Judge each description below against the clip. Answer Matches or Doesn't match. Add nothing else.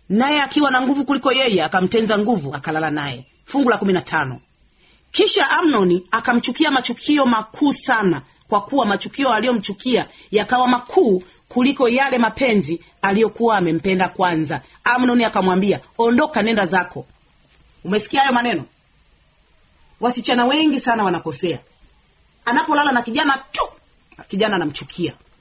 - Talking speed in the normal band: Matches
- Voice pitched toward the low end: Doesn't match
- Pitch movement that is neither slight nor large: Doesn't match